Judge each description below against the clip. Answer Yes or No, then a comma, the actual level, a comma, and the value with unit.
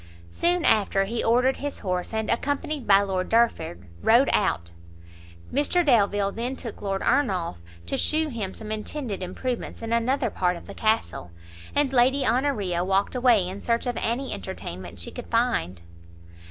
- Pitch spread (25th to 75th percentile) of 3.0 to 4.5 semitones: No, average, 5.3 semitones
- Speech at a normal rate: Yes, average, 160 wpm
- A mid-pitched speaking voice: No, high, 225 Hz